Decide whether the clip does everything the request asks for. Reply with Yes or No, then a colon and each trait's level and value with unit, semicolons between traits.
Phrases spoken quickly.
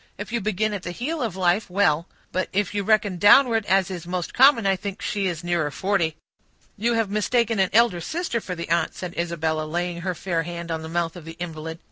Yes: fast, 225 wpm